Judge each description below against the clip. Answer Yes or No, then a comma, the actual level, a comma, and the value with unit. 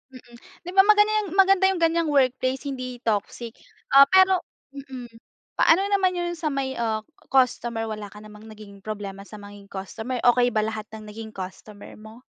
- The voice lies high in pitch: Yes, high, 245 Hz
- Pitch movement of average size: No, wide, 6.5 semitones